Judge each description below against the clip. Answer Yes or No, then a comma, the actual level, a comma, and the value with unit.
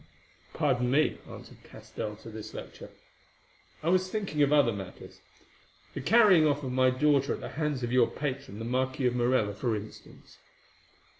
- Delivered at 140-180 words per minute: Yes, average, 165 wpm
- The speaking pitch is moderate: No, low, 130 Hz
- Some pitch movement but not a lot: Yes, average, 3.9 semitones